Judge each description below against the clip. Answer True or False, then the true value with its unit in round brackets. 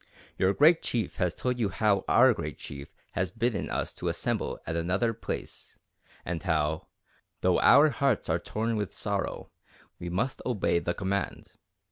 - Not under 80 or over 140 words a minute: False (160 wpm)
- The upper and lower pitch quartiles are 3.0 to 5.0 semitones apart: False (5.5 semitones)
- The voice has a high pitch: False (100 Hz)